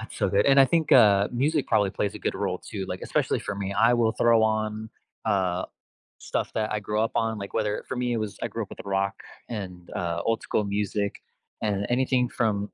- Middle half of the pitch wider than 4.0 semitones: No, narrow, 2.4 semitones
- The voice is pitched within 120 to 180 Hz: No, low, 105 Hz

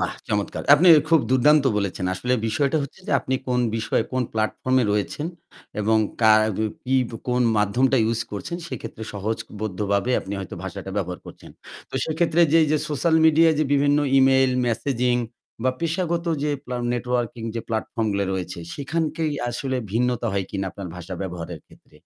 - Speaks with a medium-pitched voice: No, low, 125 Hz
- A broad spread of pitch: Yes, wide, 5.7 semitones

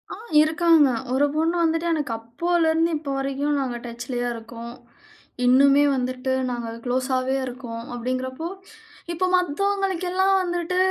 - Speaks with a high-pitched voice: Yes, very high, 275 Hz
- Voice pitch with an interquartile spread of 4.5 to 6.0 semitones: Yes, average, 5.0 semitones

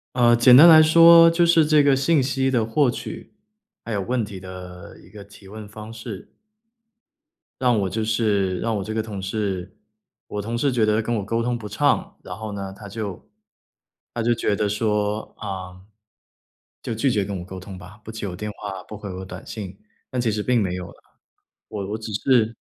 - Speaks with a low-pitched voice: Yes, low, 110 Hz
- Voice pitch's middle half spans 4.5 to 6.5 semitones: No, average, 3.3 semitones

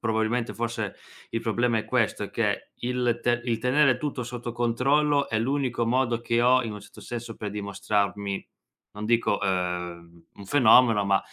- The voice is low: Yes, low, 115 Hz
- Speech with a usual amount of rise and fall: Yes, average, 3.0 semitones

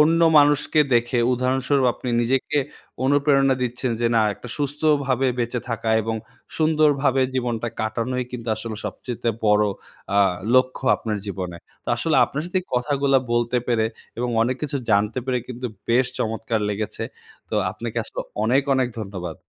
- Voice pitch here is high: No, low, 125 Hz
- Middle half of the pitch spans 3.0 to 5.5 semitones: Yes, average, 3.3 semitones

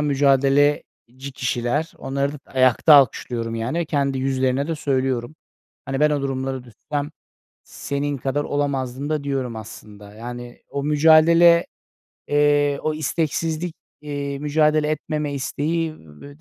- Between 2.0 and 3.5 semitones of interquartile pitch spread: Yes, narrow, 2.5 semitones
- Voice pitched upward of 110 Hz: Yes, medium, 140 Hz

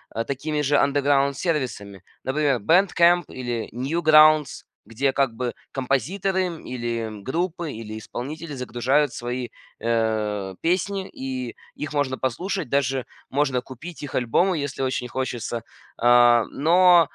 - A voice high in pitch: No, low, 135 Hz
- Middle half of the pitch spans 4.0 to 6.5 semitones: Yes, average, 4.4 semitones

